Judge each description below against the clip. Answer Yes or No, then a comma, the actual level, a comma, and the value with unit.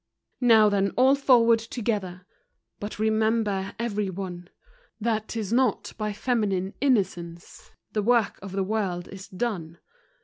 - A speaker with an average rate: No, slow, 130 wpm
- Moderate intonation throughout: Yes, average, 3.2 semitones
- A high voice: Yes, high, 210 Hz